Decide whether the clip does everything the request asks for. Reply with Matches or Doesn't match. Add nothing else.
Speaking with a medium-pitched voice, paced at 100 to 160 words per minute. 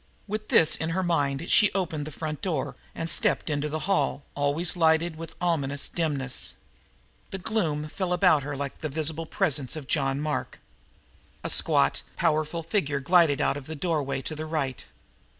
Doesn't match